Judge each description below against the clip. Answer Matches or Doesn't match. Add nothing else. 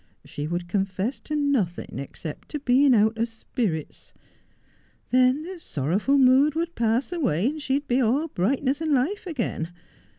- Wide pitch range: Matches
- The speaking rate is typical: Matches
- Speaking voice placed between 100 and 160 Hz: Doesn't match